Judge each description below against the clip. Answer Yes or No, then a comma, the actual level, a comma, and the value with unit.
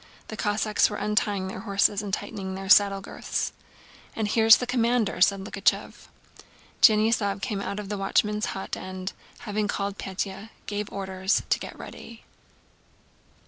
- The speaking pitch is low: No, high, 205 Hz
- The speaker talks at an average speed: Yes, average, 145 wpm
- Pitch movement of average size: No, narrow, 1.7 semitones